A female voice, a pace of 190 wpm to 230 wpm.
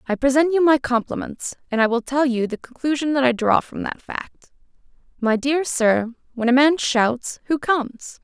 Yes: female; average, 195 wpm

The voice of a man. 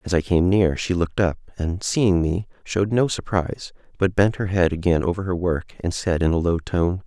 Yes: male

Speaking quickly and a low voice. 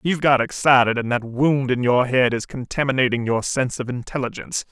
No: average, 190 wpm; low, 130 Hz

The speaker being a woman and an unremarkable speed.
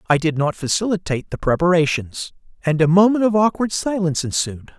No: male; average, 165 wpm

